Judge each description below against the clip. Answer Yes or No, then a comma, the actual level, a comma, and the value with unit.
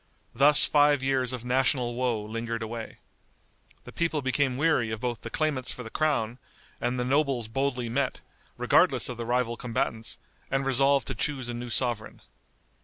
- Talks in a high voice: No, low, 125 Hz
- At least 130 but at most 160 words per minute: No, average, 170 wpm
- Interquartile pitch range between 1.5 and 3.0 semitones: Yes, narrow, 2.6 semitones